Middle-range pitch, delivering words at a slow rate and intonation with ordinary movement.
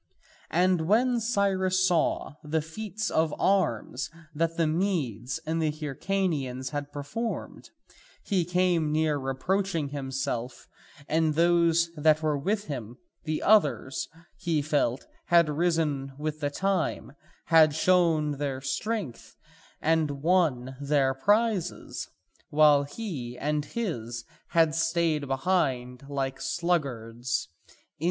Yes: medium, 155 Hz; slow, 115 wpm; average, 4.3 semitones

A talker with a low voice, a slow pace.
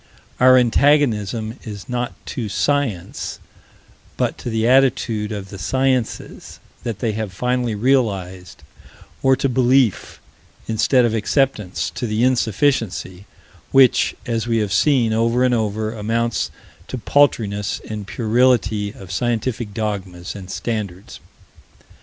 Yes: low, 115 Hz; slow, 125 wpm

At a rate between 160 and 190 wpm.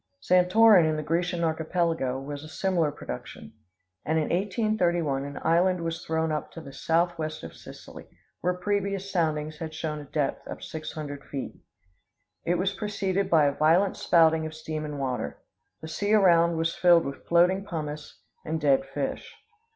Yes: average, 165 wpm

